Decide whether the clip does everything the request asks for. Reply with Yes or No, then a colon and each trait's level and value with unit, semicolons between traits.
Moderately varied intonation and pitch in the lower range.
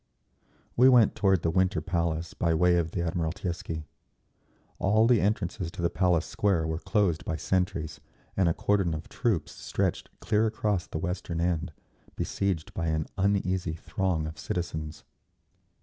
Yes: average, 3.2 semitones; very low, 90 Hz